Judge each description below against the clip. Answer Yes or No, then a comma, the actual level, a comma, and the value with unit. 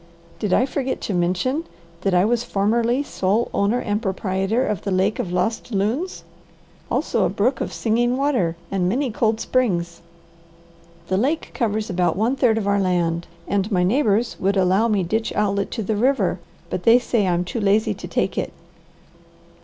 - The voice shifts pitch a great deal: No, average, 4.0 semitones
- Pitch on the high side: Yes, high, 210 Hz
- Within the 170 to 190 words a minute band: Yes, average, 175 wpm